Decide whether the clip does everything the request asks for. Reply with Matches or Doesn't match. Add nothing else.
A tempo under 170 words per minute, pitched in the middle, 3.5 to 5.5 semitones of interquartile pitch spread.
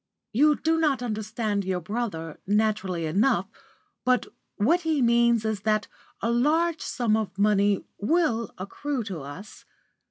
Doesn't match